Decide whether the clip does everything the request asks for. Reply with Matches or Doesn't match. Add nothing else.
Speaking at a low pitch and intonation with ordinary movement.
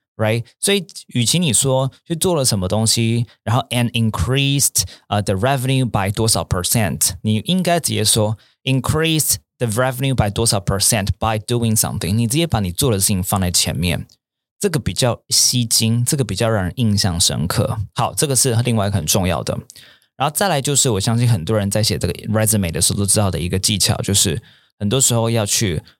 Matches